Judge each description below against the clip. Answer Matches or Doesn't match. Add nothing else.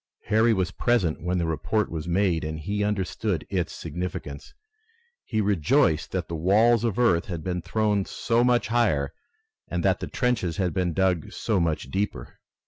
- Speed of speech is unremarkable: Matches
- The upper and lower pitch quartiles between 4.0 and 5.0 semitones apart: Matches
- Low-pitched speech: Matches